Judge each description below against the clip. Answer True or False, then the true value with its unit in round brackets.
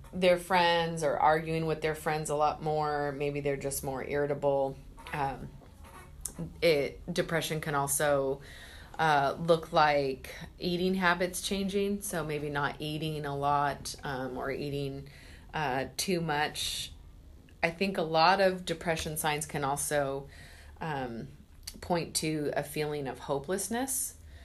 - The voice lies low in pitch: False (150 Hz)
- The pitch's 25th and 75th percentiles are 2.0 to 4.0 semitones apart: True (3.2 semitones)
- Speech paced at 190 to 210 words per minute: False (135 wpm)